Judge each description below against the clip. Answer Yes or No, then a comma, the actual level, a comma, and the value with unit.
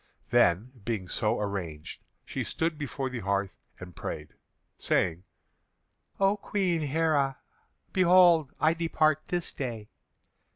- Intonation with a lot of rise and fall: Yes, wide, 8.3 semitones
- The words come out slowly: Yes, slow, 115 wpm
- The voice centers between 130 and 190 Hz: Yes, low, 135 Hz